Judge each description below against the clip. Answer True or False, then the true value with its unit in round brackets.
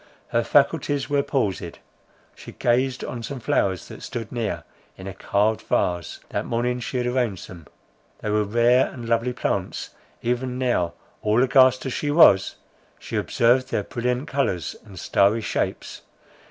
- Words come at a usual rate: True (155 wpm)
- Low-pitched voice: True (120 Hz)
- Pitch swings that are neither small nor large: True (3.6 semitones)